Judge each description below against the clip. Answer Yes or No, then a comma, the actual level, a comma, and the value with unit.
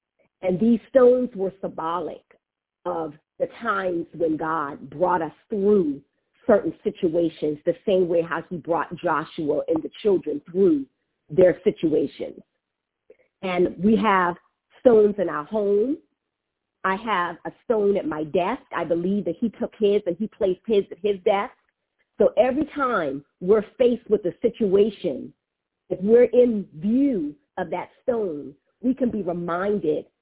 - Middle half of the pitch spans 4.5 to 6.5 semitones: Yes, average, 5.1 semitones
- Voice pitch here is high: Yes, high, 195 Hz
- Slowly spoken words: No, average, 145 wpm